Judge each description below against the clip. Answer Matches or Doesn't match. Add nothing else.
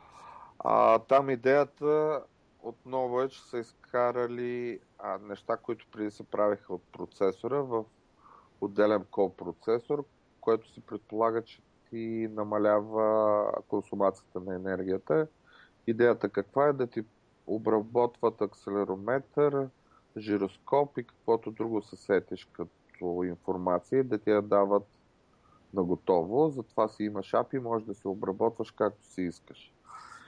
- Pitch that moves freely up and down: Doesn't match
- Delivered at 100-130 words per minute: Matches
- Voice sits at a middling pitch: Doesn't match